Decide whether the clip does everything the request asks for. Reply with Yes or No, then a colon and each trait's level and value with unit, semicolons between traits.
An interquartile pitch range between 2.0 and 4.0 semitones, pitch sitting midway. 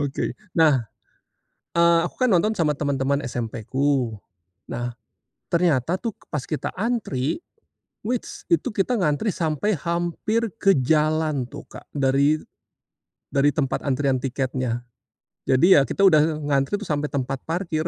No: average, 4.4 semitones; medium, 150 Hz